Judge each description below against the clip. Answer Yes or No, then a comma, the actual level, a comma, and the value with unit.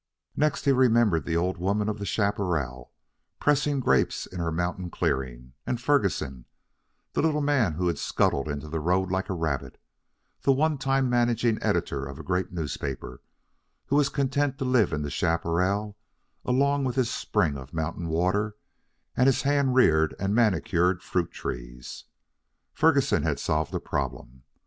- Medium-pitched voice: No, very low, 95 Hz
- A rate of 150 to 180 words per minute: Yes, average, 160 wpm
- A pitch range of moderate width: No, wide, 8.1 semitones